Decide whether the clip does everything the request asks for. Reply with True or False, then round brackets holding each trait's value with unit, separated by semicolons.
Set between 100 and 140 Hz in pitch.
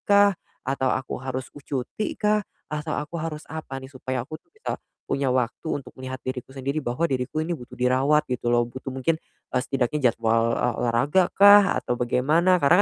True (135 Hz)